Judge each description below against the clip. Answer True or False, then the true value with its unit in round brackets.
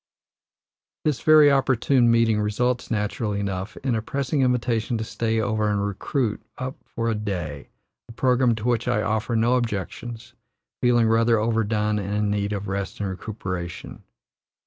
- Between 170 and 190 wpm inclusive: False (155 wpm)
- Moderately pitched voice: False (110 Hz)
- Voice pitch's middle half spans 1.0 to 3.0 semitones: True (2.7 semitones)